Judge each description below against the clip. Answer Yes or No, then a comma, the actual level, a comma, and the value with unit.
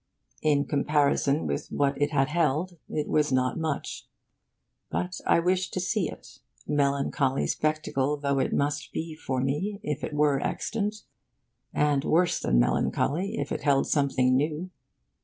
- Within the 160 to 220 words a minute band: No, average, 150 wpm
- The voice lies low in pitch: No, medium, 150 Hz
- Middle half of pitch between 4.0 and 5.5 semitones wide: No, average, 3.0 semitones